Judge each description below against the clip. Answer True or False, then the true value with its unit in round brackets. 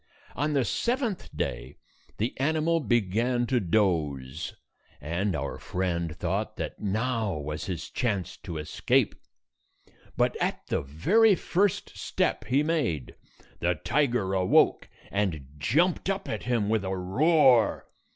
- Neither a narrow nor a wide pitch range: False (8.9 semitones)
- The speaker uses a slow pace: True (130 wpm)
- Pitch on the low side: True (105 Hz)